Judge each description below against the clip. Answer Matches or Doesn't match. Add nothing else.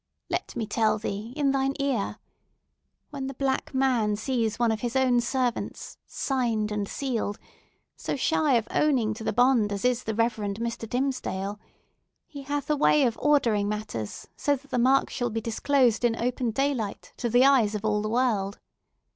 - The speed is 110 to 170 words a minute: Doesn't match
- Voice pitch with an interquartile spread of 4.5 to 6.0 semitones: Doesn't match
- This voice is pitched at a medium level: Doesn't match